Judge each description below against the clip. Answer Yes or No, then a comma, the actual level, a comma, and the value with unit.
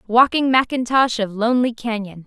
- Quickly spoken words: No, slow, 135 wpm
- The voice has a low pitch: No, high, 235 Hz